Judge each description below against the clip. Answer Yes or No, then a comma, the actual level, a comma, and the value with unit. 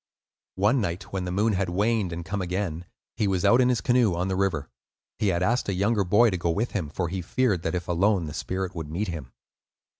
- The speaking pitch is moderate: No, very low, 95 Hz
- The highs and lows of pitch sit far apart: No, average, 3.3 semitones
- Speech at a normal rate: No, fast, 240 wpm